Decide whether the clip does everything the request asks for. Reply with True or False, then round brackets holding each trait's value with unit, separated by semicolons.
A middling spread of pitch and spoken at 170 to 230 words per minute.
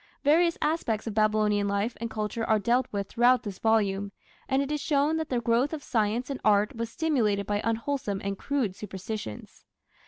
True (4.5 semitones; 185 wpm)